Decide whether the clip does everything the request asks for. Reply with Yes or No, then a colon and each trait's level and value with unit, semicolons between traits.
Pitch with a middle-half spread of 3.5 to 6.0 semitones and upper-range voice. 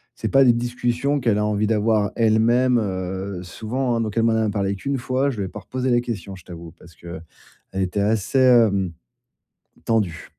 No: average, 3.8 semitones; low, 110 Hz